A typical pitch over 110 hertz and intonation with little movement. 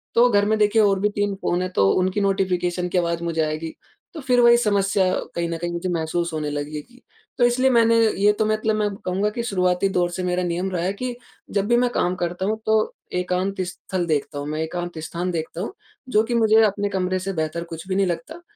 No: medium, 185 Hz; average, 3.6 semitones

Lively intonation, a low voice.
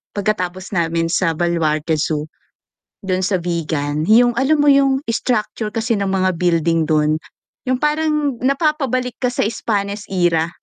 No: wide, 7.0 semitones; high, 195 Hz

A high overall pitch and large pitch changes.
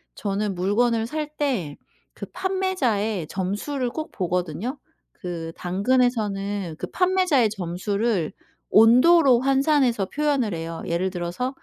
Yes: high, 220 Hz; wide, 6.7 semitones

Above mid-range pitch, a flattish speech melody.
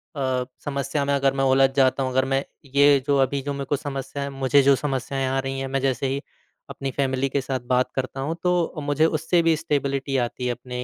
No: low, 135 Hz; narrow, 1.2 semitones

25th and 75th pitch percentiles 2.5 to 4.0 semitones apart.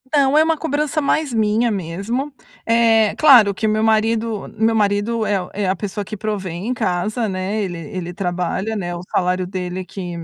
Yes: average, 3.6 semitones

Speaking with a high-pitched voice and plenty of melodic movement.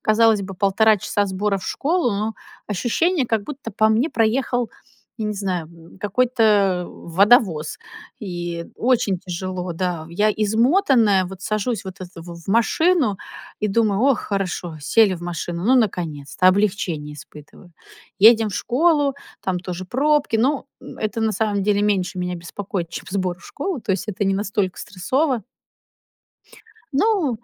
No: high, 205 Hz; average, 4.1 semitones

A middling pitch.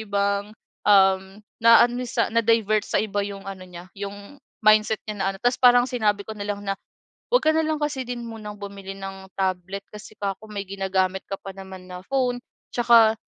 No: high, 205 Hz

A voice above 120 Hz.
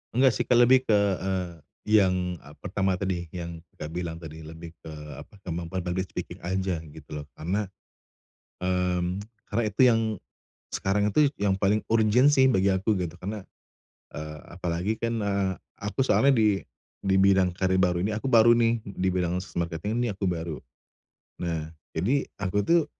No: very low, 95 Hz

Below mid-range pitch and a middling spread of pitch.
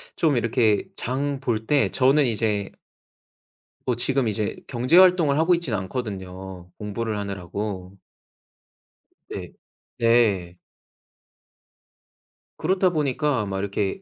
No: low, 115 Hz; wide, 5.7 semitones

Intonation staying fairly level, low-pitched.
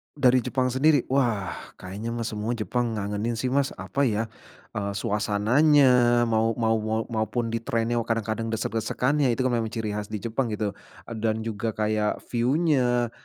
Yes: narrow, 2.3 semitones; low, 115 Hz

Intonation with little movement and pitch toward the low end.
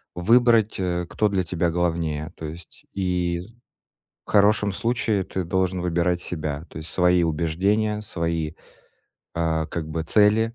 No: average, 3.6 semitones; very low, 90 Hz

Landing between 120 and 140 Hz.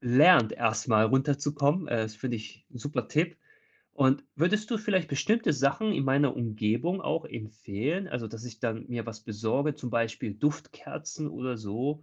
Yes: low, 135 Hz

